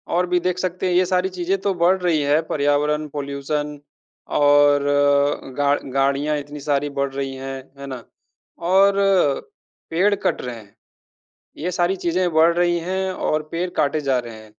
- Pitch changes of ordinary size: Yes, average, 4.1 semitones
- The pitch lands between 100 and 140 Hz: No, medium, 150 Hz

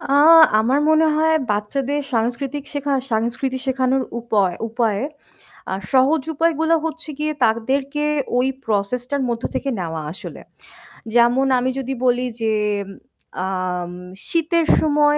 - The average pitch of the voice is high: Yes, very high, 260 Hz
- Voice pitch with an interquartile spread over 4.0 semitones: Yes, average, 4.7 semitones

